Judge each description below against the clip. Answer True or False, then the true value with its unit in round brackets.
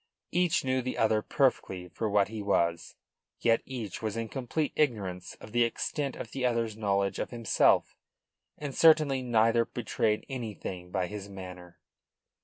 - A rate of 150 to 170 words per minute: True (155 wpm)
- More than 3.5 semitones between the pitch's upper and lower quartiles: True (4.4 semitones)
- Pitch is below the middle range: True (110 Hz)